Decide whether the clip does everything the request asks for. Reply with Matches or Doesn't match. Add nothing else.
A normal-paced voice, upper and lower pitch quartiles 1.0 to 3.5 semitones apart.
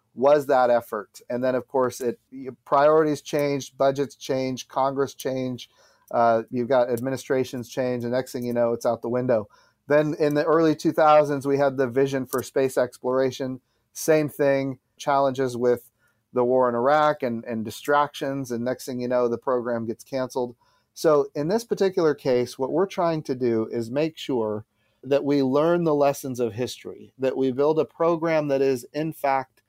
Matches